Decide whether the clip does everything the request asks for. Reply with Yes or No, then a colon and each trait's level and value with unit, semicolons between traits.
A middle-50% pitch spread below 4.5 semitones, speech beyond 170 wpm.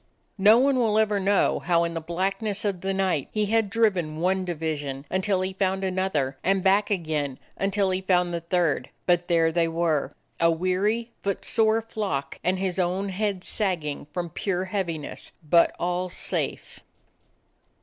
No: average, 2.9 semitones; average, 165 wpm